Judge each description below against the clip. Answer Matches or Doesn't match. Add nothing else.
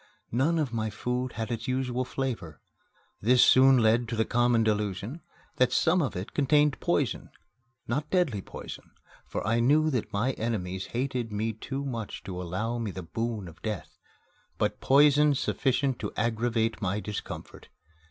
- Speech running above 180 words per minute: Doesn't match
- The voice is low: Matches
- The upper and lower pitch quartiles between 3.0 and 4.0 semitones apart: Matches